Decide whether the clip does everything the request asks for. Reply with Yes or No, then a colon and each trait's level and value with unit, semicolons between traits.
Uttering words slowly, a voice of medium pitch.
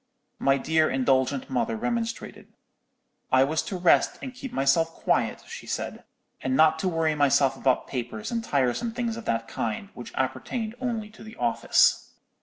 No: average, 165 wpm; medium, 160 Hz